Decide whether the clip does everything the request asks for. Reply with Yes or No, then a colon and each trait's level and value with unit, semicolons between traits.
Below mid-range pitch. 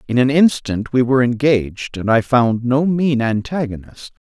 Yes: low, 125 Hz